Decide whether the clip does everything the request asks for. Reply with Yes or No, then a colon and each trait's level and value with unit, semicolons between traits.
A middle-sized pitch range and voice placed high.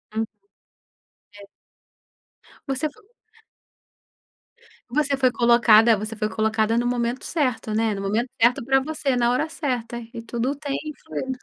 Yes: average, 3.2 semitones; high, 240 Hz